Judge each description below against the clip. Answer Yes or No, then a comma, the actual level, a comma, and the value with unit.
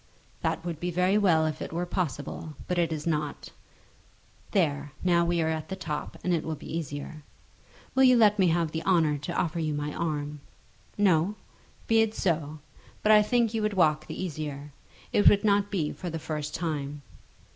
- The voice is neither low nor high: Yes, medium, 165 Hz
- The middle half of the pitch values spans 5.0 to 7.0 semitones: No, average, 3.8 semitones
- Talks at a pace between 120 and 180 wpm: No, average, 195 wpm